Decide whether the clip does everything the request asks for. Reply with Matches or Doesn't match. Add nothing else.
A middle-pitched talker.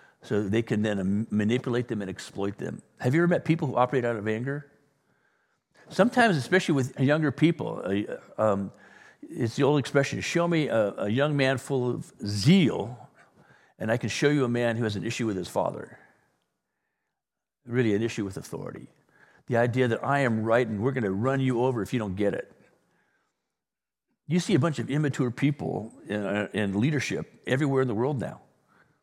Doesn't match